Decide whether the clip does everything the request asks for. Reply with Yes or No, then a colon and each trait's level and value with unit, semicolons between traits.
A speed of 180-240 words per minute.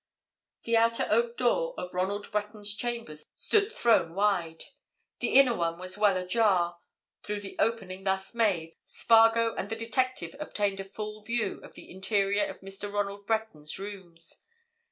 No: average, 155 wpm